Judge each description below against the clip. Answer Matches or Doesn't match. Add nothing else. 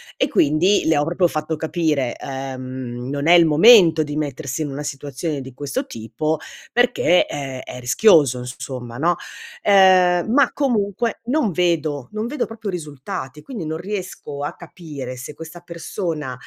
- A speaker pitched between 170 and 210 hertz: Doesn't match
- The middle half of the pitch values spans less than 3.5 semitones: Doesn't match